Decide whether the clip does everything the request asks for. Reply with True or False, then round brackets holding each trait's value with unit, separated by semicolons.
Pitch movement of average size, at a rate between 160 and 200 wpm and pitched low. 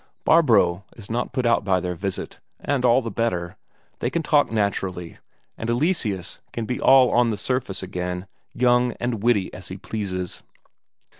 True (4.9 semitones; 165 wpm; 110 Hz)